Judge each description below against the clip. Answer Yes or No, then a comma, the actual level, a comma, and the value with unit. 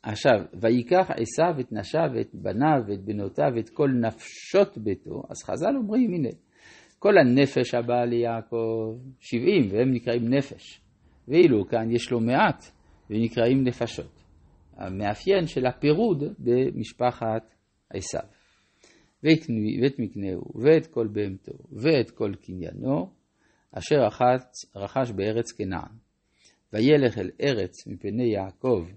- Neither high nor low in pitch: No, low, 115 Hz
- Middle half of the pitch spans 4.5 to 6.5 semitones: No, average, 4.1 semitones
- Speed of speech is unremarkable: Yes, average, 115 wpm